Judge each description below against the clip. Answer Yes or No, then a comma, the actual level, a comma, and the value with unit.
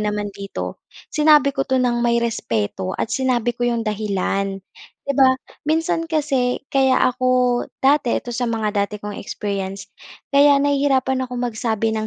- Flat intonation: No, average, 4.3 semitones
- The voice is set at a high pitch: Yes, high, 240 Hz